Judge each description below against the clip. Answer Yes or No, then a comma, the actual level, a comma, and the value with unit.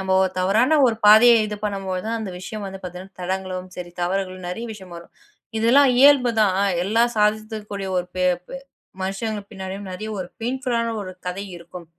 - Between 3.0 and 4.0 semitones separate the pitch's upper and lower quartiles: Yes, average, 3.3 semitones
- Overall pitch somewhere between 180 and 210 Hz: Yes, high, 195 Hz